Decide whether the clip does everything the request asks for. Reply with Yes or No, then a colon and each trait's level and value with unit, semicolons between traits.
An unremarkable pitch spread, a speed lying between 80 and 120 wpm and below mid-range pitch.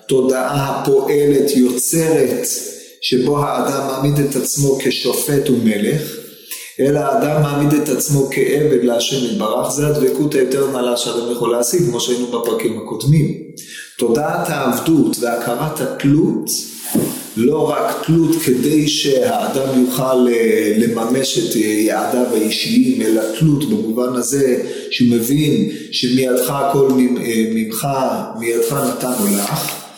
Yes: average, 3.4 semitones; average, 110 wpm; low, 130 Hz